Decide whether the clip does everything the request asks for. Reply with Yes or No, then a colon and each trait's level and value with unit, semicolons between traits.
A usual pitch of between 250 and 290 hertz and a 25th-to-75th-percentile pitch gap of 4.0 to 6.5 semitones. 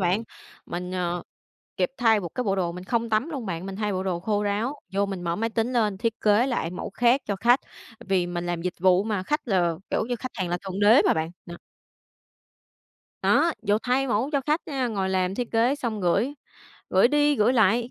No: high, 205 Hz; average, 4.5 semitones